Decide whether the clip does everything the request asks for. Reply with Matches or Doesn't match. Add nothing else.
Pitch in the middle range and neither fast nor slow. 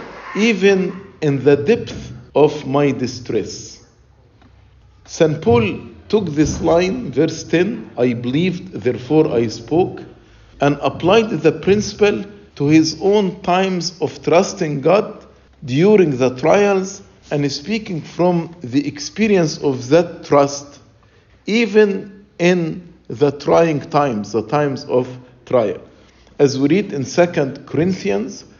Doesn't match